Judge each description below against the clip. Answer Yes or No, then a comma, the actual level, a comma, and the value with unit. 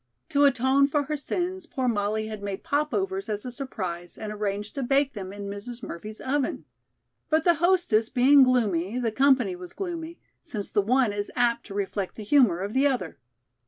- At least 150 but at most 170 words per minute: No, average, 190 wpm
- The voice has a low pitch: No, high, 245 Hz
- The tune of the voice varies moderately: No, wide, 5.7 semitones